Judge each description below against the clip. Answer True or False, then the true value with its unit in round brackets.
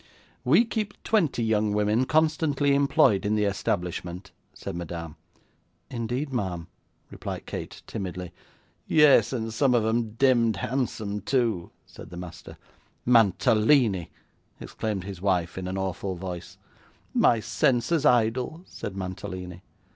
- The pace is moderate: False (125 wpm)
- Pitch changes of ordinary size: False (5.7 semitones)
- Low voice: True (110 Hz)